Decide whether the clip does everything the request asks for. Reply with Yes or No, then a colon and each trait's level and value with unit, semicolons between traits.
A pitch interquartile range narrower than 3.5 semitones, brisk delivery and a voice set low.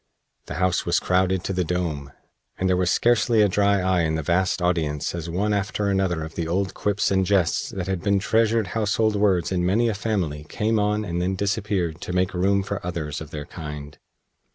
Yes: average, 3.0 semitones; fast, 210 wpm; very low, 95 Hz